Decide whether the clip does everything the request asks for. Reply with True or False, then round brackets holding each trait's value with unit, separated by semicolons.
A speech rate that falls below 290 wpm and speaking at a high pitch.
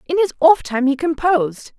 True (200 wpm; 300 Hz)